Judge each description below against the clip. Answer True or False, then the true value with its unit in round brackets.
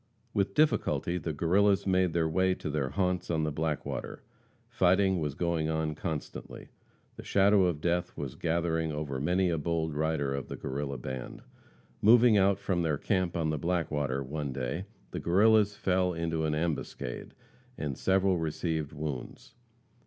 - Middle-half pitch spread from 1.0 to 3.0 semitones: False (3.7 semitones)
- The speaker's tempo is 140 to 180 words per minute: True (160 wpm)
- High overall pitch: False (80 Hz)